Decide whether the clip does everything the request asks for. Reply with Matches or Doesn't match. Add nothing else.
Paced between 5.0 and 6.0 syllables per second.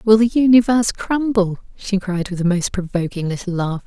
Matches